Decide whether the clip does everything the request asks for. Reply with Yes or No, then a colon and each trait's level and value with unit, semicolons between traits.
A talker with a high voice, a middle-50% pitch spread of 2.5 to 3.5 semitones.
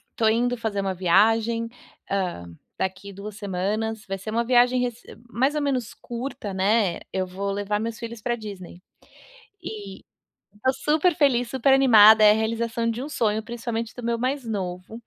Yes: high, 225 Hz; average, 3.1 semitones